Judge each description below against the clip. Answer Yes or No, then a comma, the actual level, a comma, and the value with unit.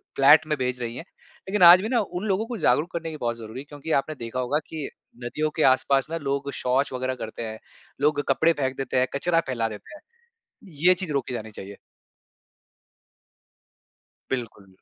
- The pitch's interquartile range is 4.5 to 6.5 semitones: Yes, average, 4.8 semitones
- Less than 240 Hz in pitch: Yes, medium, 140 Hz